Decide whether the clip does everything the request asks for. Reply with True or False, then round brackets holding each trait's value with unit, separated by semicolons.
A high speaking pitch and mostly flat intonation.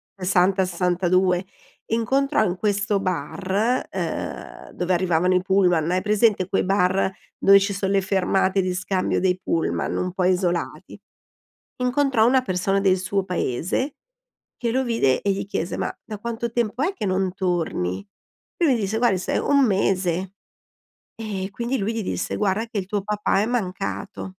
False (195 Hz; 3.1 semitones)